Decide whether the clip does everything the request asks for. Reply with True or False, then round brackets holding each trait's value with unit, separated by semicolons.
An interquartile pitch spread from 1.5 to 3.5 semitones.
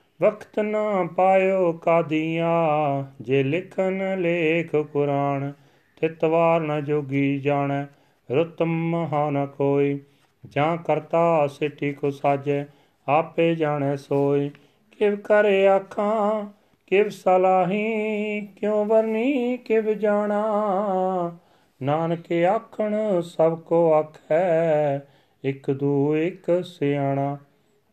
False (5.1 semitones)